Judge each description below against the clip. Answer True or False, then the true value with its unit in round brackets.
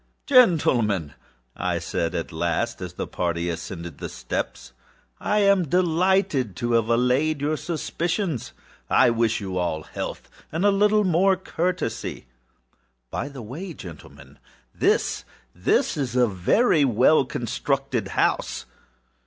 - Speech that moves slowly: True (120 wpm)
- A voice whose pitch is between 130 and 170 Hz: True (135 Hz)